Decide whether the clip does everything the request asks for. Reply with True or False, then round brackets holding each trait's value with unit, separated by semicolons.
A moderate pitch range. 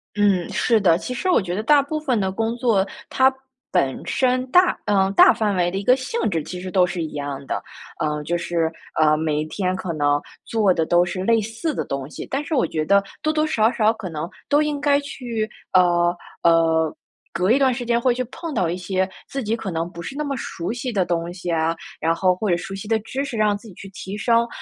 False (5.9 semitones)